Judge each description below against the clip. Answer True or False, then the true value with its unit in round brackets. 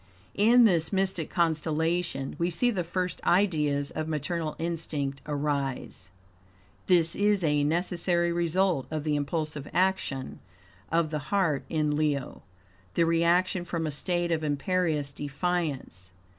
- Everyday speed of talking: False (130 wpm)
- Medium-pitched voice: True (165 Hz)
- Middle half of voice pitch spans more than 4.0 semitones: False (3.2 semitones)